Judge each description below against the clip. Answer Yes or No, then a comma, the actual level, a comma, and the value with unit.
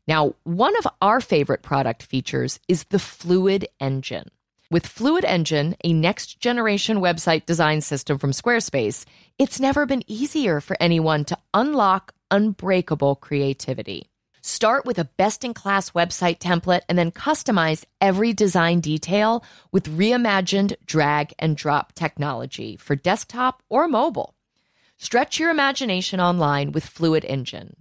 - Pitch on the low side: No, medium, 175 Hz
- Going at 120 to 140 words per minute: Yes, slow, 135 wpm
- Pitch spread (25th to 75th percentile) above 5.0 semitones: Yes, wide, 5.6 semitones